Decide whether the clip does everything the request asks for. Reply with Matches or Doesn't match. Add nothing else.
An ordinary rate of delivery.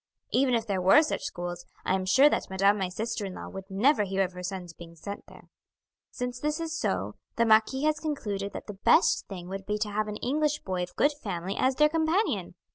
Doesn't match